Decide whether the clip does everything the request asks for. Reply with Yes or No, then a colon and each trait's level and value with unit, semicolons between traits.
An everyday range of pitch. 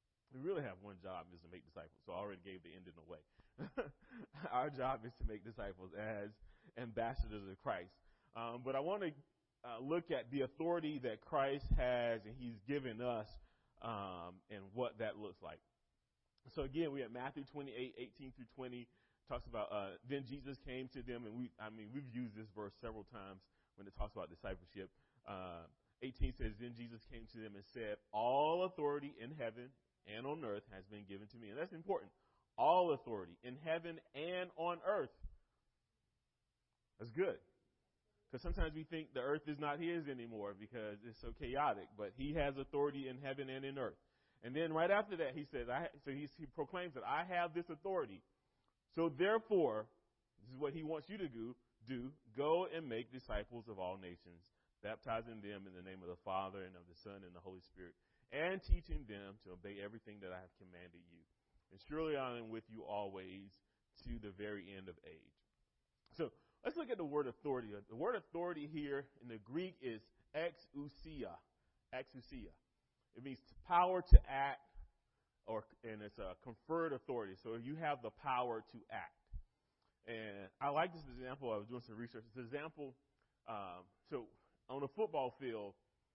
No: wide, 5.8 semitones